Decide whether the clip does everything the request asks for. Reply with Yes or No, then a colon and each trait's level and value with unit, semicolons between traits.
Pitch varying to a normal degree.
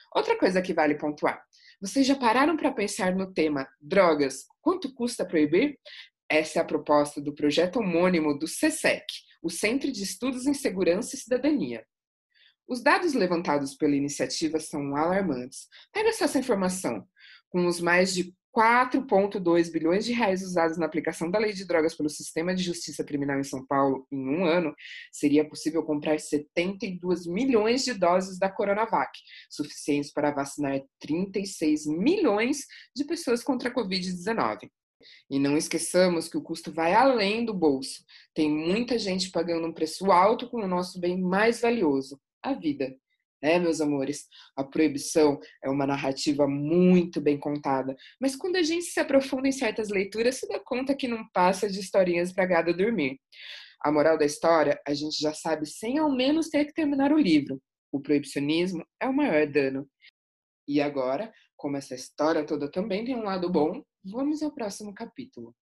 No: wide, 7.5 semitones